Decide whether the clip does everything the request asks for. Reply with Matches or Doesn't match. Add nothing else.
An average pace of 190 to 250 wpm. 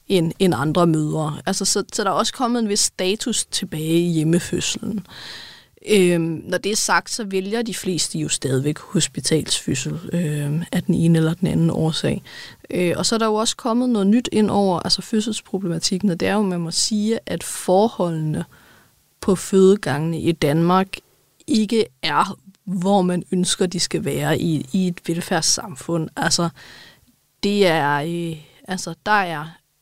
Doesn't match